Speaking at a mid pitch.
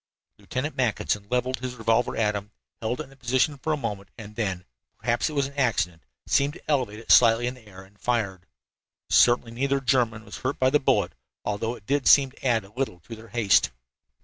No: low, 120 Hz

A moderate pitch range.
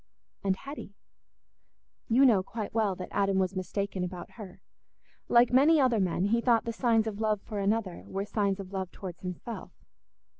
Yes: average, 3.3 semitones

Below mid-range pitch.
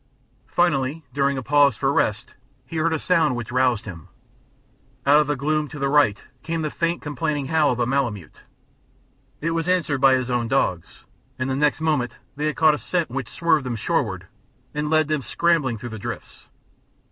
No: medium, 145 Hz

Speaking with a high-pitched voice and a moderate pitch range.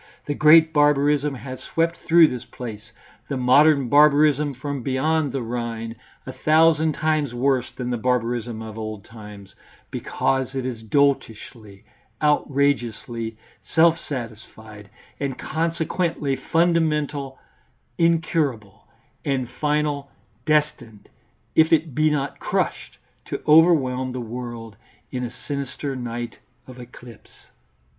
No: low, 135 Hz; average, 4.1 semitones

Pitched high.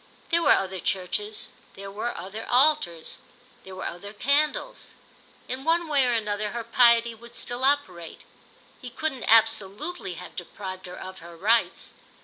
Yes: high, 225 Hz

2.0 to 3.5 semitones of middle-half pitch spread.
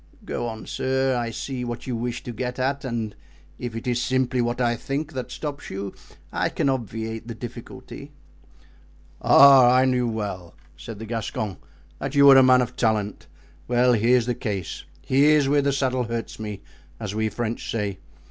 Yes: narrow, 2.6 semitones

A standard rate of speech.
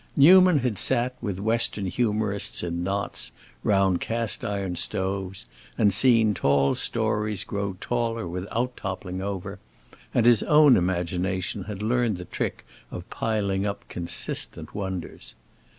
No: slow, 130 wpm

